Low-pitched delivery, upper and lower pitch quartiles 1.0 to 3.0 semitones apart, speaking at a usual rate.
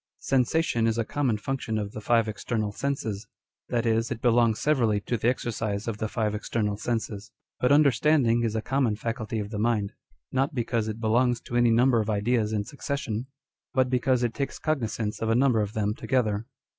Yes: low, 115 Hz; average, 2.7 semitones; average, 195 wpm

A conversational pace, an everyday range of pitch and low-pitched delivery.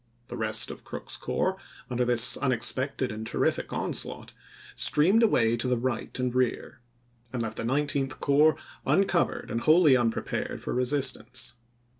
Yes: average, 145 wpm; average, 3.3 semitones; low, 125 Hz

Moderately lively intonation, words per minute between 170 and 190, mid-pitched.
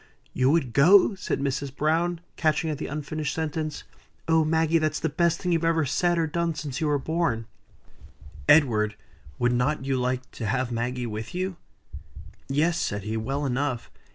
Yes: average, 4.2 semitones; average, 175 wpm; medium, 150 Hz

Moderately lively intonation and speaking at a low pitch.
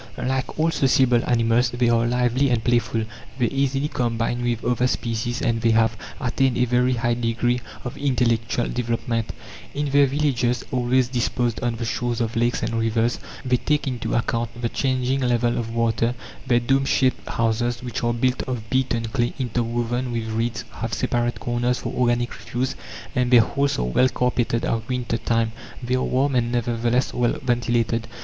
No: narrow, 1.4 semitones; low, 120 Hz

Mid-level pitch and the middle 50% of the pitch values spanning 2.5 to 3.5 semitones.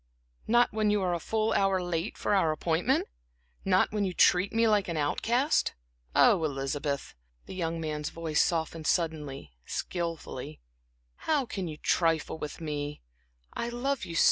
No: medium, 170 Hz; average, 4.9 semitones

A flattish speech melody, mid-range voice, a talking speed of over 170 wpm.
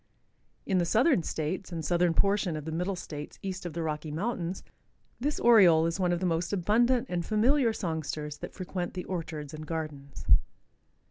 No: average, 3.6 semitones; medium, 175 Hz; average, 180 wpm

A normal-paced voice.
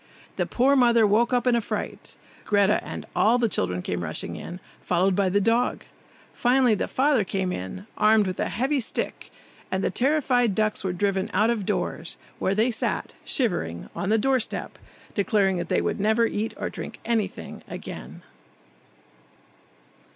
Yes: average, 165 wpm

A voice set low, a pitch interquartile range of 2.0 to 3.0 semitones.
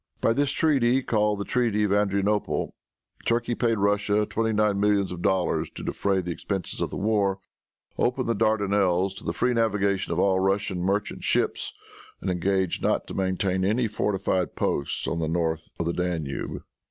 Yes: low, 100 Hz; narrow, 2.5 semitones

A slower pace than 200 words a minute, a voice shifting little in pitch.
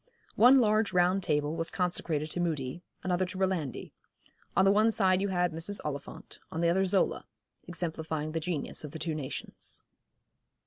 No: average, 170 wpm; average, 3.4 semitones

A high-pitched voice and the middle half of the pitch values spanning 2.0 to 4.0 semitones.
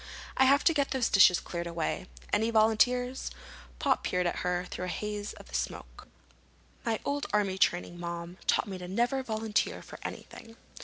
No: high, 210 Hz; average, 5.2 semitones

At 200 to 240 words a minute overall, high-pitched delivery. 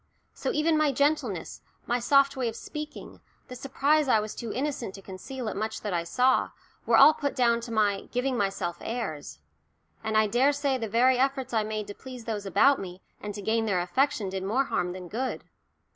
Yes: fast, 205 wpm; high, 235 Hz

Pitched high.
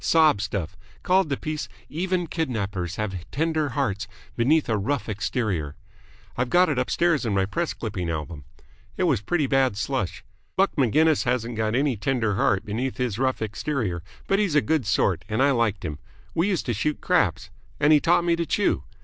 No: low, 125 Hz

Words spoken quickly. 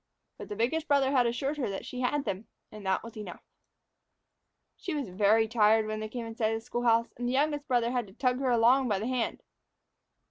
Yes: fast, 235 wpm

